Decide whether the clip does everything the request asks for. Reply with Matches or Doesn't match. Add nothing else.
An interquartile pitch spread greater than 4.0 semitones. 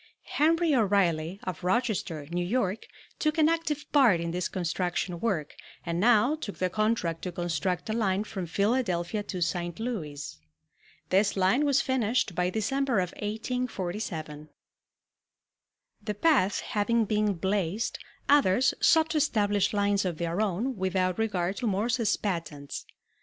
Matches